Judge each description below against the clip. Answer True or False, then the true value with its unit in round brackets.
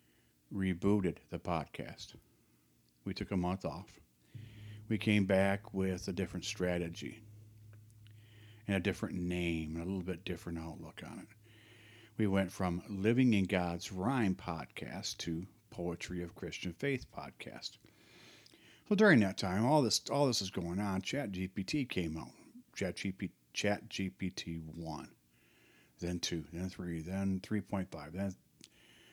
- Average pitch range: True (3.5 semitones)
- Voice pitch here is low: True (95 Hz)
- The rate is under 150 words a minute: True (140 wpm)